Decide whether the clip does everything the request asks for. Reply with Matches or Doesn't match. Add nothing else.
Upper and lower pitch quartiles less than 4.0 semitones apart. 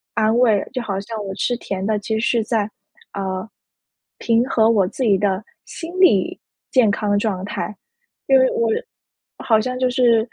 Matches